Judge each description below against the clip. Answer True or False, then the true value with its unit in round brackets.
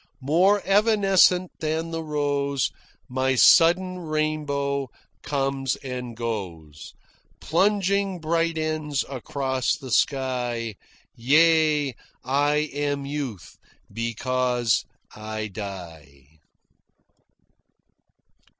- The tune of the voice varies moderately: True (4.7 semitones)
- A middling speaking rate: False (75 wpm)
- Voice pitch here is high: False (140 Hz)